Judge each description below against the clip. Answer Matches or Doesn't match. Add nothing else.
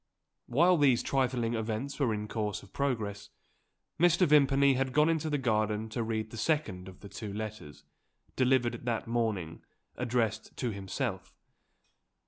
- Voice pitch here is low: Matches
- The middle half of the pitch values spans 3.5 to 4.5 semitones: Matches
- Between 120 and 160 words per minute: Matches